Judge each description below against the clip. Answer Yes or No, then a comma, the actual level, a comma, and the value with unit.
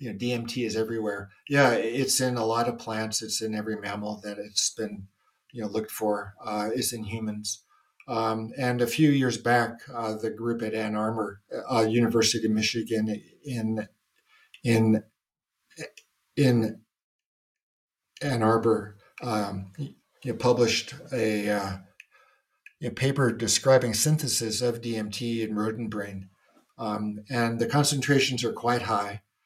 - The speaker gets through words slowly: No, average, 145 wpm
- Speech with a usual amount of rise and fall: No, narrow, 2.2 semitones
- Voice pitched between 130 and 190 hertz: No, low, 110 Hz